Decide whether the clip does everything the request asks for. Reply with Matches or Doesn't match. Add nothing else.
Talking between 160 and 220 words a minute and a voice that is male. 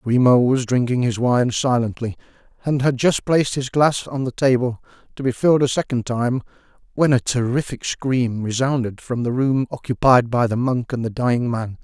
Matches